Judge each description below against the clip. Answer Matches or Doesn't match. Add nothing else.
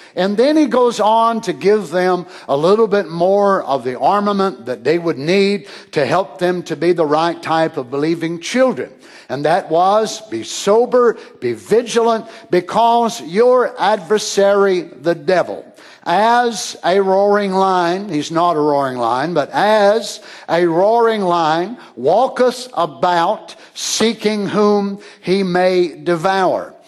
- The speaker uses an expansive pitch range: Doesn't match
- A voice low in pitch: Doesn't match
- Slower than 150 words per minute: Matches